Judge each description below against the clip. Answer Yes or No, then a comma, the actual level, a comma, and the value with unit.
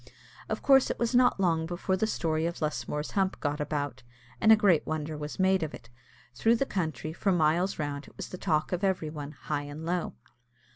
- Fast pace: Yes, fast, 210 wpm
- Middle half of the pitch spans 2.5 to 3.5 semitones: No, average, 4.0 semitones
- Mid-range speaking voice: Yes, medium, 160 Hz